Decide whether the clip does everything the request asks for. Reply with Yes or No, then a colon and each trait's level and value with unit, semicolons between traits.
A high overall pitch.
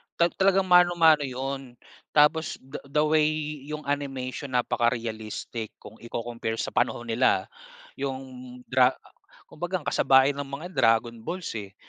No: low, 135 Hz